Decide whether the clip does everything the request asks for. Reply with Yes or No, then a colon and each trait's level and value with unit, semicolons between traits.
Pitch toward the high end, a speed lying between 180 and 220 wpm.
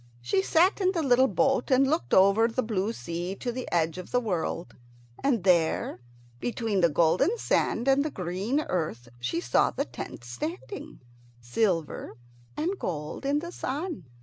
No: high, 215 Hz; average, 165 wpm